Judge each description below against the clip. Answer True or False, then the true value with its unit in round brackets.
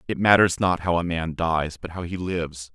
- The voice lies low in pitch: True (85 Hz)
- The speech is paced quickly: True (240 wpm)